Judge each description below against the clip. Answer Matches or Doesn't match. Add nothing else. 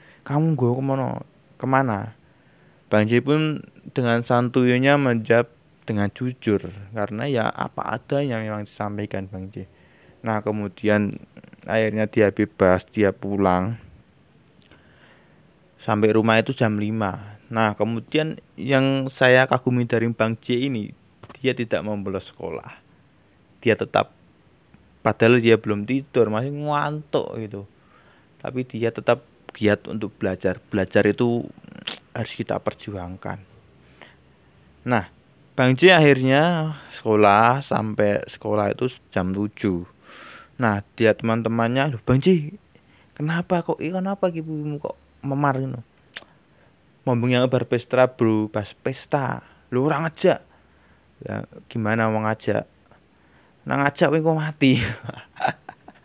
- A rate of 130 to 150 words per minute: Doesn't match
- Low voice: Matches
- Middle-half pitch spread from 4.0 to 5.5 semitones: Matches